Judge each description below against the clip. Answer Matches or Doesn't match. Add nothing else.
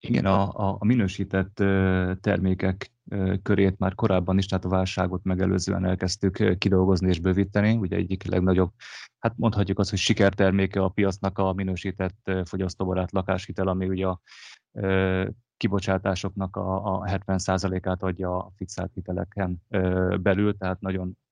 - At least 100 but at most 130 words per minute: Matches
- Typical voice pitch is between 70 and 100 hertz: Matches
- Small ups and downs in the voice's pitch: Matches